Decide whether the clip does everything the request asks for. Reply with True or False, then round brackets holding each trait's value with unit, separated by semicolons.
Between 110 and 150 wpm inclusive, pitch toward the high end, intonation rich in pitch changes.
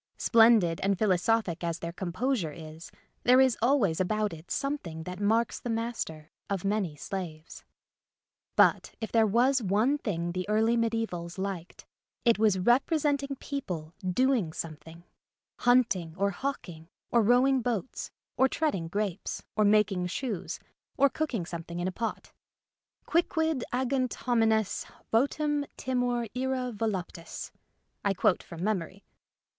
True (140 wpm; 215 Hz; 5.9 semitones)